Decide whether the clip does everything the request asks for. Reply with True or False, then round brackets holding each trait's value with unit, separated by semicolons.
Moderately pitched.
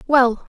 False (255 Hz)